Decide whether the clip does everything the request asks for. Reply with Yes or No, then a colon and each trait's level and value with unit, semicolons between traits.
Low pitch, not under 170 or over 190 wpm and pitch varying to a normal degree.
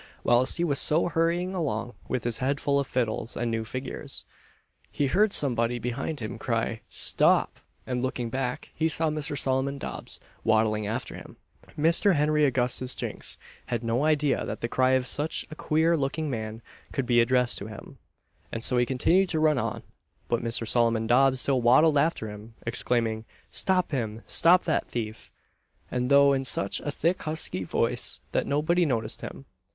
Yes: low, 130 Hz; average, 175 wpm; average, 4.6 semitones